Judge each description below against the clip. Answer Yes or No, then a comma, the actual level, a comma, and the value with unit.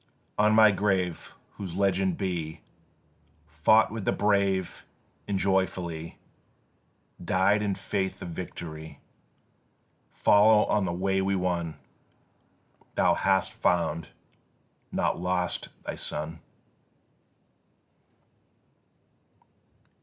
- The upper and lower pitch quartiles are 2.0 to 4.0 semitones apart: Yes, narrow, 2.6 semitones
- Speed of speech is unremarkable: No, slow, 90 wpm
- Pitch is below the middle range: Yes, very low, 95 Hz